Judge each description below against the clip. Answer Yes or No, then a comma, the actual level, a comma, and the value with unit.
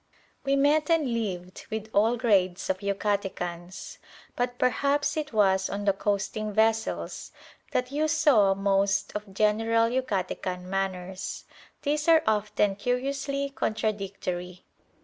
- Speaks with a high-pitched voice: Yes, high, 210 Hz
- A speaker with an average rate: No, slow, 120 wpm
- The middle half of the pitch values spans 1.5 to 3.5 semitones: No, average, 4.8 semitones